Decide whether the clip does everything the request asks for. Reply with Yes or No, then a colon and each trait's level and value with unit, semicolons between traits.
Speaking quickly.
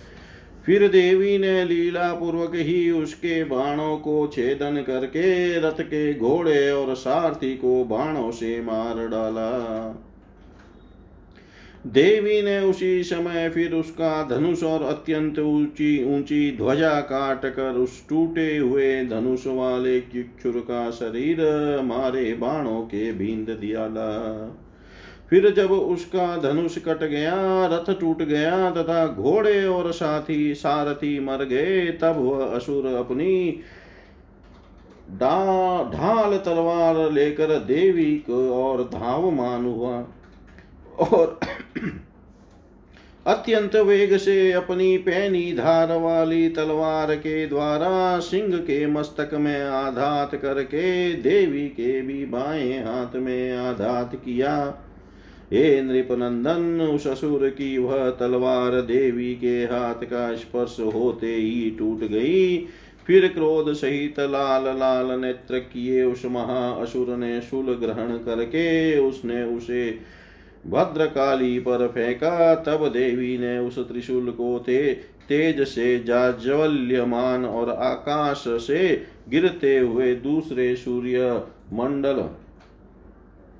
No: slow, 110 wpm